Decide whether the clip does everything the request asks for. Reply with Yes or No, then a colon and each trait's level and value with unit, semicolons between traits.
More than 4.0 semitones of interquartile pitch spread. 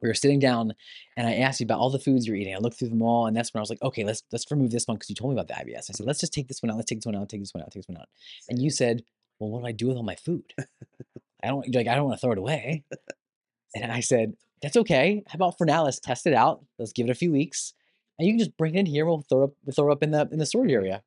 Yes: average, 4.4 semitones